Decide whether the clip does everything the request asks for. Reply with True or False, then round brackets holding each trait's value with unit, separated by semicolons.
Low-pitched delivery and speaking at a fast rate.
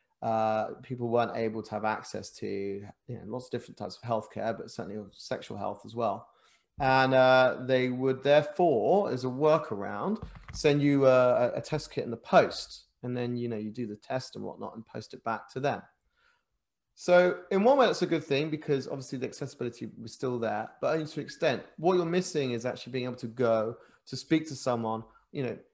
True (130 Hz; 210 wpm)